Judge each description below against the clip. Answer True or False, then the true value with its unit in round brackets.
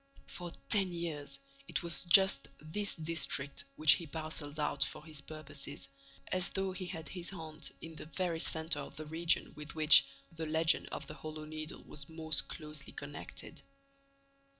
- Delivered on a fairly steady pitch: True (1.9 semitones)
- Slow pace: False (165 wpm)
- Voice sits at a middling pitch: True (160 Hz)